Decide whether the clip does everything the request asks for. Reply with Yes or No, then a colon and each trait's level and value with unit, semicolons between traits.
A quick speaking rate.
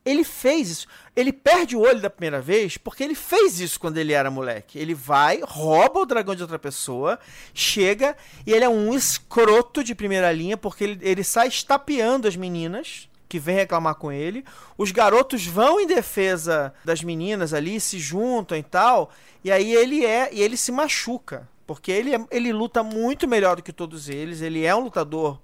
No: average, 190 wpm